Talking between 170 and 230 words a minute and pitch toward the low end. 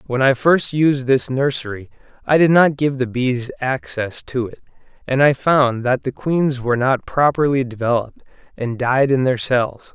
Yes: average, 180 wpm; low, 130 Hz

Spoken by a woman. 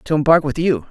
No: male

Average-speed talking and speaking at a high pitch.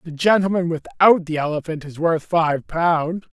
No: average, 160 wpm; medium, 165 Hz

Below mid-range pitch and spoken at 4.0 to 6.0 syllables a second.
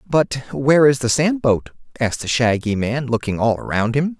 Yes: low, 130 Hz; 5.2 syllables/s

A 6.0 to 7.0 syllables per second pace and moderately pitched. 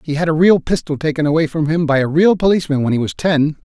Yes: 6.5 syllables/s; medium, 155 Hz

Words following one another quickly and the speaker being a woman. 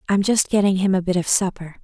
Yes: fast, 260 wpm; female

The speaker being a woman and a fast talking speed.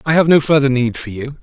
No: male; fast, 295 wpm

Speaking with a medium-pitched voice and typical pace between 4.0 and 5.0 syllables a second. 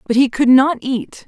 No: very high, 255 Hz; 4.6 syllables/s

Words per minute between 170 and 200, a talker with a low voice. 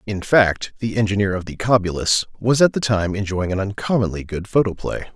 Yes: average, 185 wpm; low, 100 Hz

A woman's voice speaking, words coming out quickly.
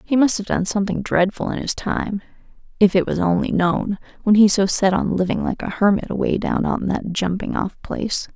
Yes: female; fast, 215 wpm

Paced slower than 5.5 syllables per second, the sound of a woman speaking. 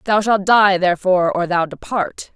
Yes: 5.0 syllables/s; female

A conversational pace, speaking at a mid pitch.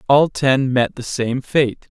No: average, 180 wpm; low, 130 Hz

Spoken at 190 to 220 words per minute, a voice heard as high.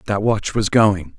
No: fast, 205 wpm; low, 100 Hz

